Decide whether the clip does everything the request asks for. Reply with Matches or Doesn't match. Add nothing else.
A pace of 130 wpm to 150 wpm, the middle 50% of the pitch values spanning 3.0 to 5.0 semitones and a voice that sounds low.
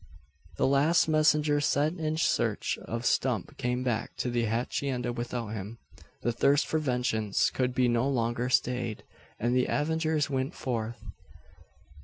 Matches